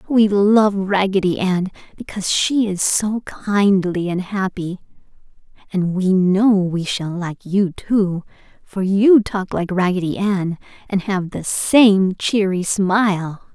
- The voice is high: Yes, high, 195 Hz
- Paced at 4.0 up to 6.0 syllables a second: No, 3.6 syllables/s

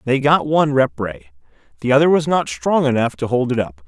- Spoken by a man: Yes, male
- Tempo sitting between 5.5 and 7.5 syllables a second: Yes, 5.8 syllables/s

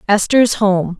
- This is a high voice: Yes, high, 205 Hz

